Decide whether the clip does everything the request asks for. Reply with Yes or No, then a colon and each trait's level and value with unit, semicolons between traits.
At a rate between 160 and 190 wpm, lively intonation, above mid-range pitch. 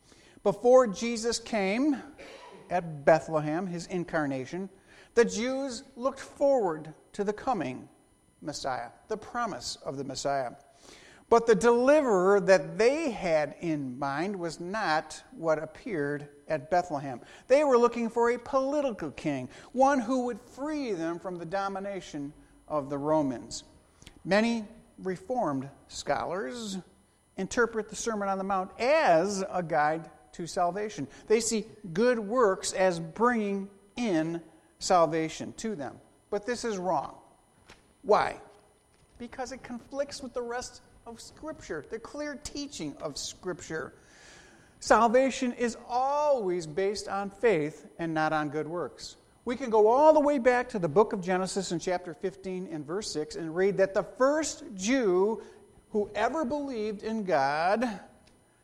No: slow, 135 wpm; wide, 6.3 semitones; high, 200 Hz